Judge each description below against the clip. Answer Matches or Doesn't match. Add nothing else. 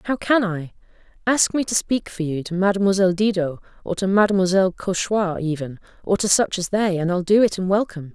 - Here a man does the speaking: Doesn't match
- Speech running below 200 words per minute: Doesn't match